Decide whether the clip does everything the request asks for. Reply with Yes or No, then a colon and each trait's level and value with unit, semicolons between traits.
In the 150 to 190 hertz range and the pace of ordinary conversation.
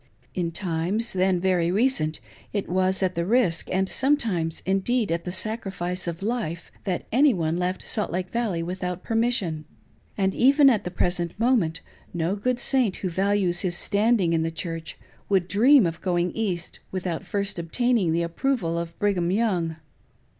Yes: medium, 185 Hz; average, 170 wpm